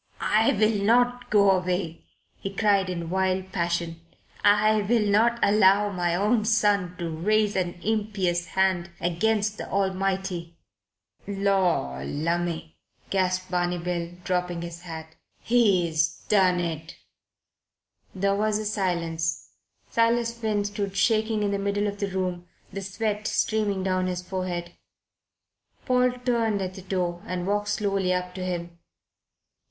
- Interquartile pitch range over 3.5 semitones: No, average, 3.0 semitones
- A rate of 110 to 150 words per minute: Yes, slow, 135 wpm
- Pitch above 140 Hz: Yes, high, 190 Hz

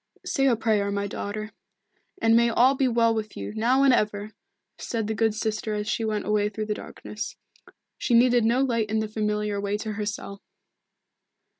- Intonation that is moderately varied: No, narrow, 1.8 semitones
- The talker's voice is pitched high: Yes, high, 220 Hz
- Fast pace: No, average, 190 wpm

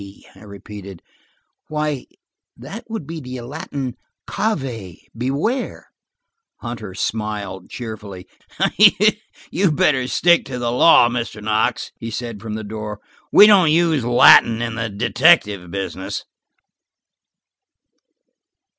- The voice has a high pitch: No, low, 120 Hz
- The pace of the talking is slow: Yes, slow, 105 wpm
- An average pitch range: No, wide, 5.8 semitones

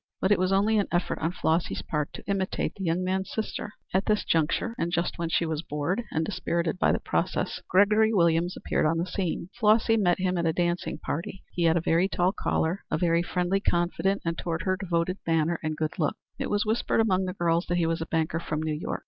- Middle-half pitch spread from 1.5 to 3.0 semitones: Yes, average, 2.7 semitones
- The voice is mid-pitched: Yes, medium, 175 Hz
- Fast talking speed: Yes, fast, 235 wpm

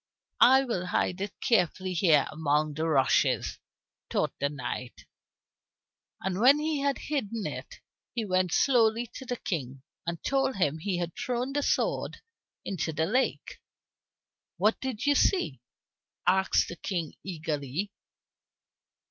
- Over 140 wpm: No, slow, 135 wpm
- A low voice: No, high, 190 Hz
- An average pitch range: No, wide, 7.6 semitones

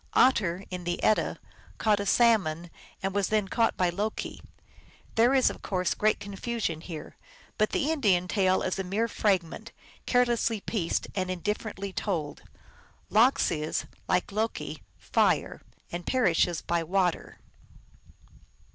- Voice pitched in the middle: No, high, 195 Hz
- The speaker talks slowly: Yes, slow, 130 wpm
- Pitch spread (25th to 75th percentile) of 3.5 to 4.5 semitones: Yes, average, 3.8 semitones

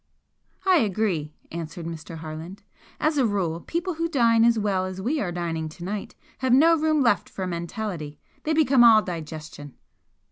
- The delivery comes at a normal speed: Yes, average, 170 wpm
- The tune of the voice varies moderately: No, wide, 7.6 semitones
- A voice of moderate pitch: No, high, 195 Hz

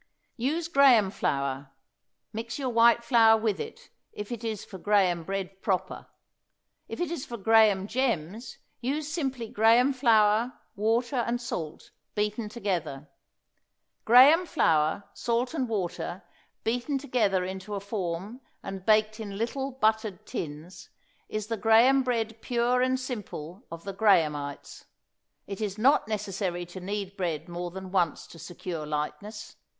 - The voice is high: Yes, high, 215 Hz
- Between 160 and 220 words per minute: No, average, 140 wpm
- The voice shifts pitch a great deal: No, average, 4.3 semitones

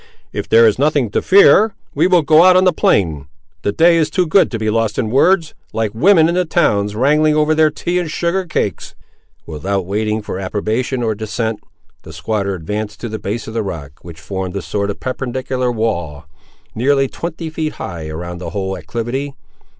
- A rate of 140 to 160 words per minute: No, average, 195 wpm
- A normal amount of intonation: No, wide, 7.6 semitones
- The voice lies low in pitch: Yes, low, 115 Hz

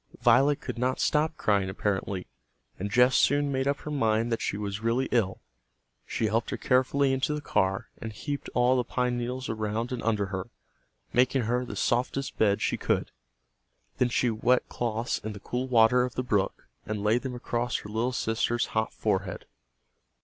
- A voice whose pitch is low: Yes, low, 120 Hz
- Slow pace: No, average, 185 wpm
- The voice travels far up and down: No, average, 2.9 semitones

